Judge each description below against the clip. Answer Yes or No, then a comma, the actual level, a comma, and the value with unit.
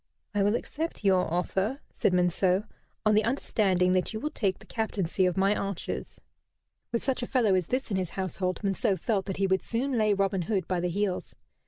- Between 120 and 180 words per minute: No, fast, 205 wpm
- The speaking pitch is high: Yes, high, 195 Hz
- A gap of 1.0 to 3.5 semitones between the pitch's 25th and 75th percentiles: Yes, average, 2.9 semitones